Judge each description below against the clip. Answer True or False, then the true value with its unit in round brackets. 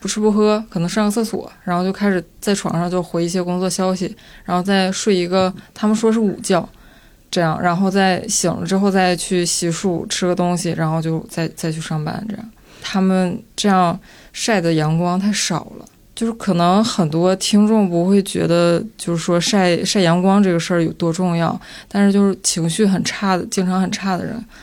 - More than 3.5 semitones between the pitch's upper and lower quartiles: False (2.7 semitones)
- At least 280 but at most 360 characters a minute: True (290 characters per minute)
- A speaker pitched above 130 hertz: True (185 Hz)